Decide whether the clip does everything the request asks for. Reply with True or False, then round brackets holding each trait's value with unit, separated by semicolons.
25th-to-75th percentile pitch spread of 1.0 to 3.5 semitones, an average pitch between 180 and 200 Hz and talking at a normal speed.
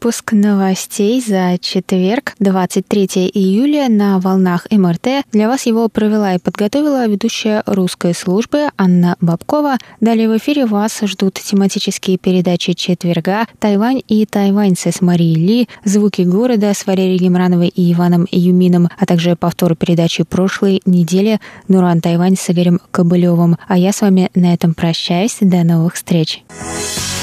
True (3.1 semitones; 190 Hz; 140 wpm)